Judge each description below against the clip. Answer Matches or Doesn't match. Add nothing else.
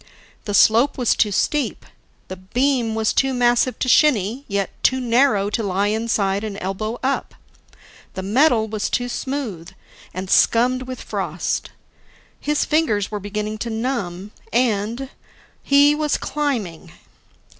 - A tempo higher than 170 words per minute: Doesn't match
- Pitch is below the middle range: Doesn't match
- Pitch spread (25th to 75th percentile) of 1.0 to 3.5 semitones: Doesn't match